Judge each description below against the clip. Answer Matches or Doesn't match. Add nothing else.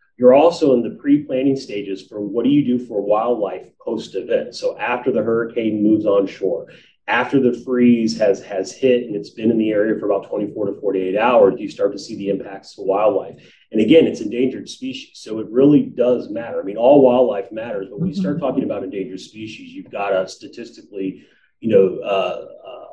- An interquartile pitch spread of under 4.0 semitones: Doesn't match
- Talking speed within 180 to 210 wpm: Matches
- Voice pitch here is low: Matches